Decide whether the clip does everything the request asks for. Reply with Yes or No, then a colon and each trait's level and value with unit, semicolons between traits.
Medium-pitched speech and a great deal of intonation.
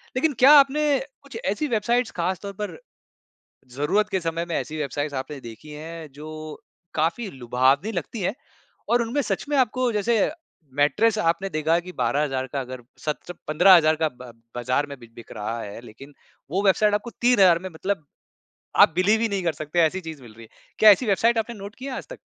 Yes: medium, 175 Hz; wide, 6.9 semitones